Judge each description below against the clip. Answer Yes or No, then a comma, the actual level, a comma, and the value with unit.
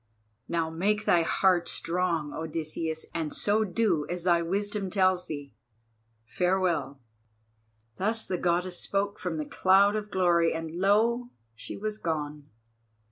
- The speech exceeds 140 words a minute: No, slow, 135 wpm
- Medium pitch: Yes, medium, 180 Hz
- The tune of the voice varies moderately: Yes, average, 3.6 semitones